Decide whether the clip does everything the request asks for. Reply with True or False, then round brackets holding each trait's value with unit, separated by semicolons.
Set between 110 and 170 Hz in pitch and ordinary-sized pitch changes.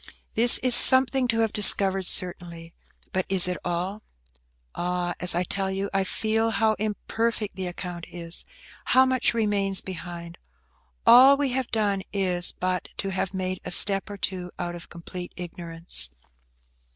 False (190 Hz; 3.7 semitones)